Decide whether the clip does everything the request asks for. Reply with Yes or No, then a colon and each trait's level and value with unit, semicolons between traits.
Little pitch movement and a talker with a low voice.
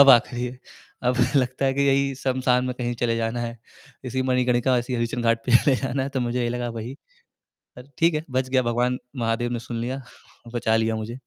Yes: narrow, 1.6 semitones; low, 125 Hz